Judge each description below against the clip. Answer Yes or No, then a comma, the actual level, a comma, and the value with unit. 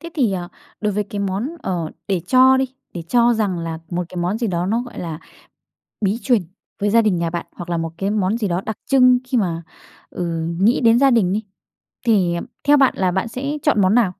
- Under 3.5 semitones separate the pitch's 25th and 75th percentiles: No, average, 5.2 semitones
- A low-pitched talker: No, high, 205 Hz